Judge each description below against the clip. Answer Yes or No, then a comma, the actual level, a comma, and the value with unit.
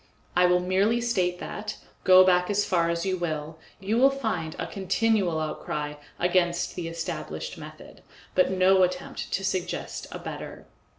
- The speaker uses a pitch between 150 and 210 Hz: Yes, medium, 185 Hz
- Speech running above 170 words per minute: No, average, 160 wpm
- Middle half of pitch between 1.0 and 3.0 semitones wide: Yes, narrow, 2.4 semitones